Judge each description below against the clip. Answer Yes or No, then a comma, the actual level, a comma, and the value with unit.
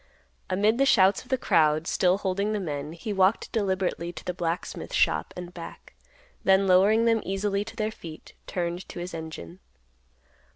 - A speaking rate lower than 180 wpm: Yes, average, 170 wpm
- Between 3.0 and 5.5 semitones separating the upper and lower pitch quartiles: Yes, average, 3.3 semitones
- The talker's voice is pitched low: No, medium, 185 Hz